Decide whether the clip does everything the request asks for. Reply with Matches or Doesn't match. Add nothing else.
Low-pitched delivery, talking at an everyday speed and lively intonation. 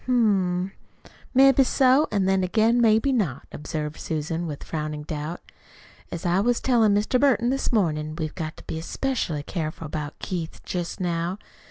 Doesn't match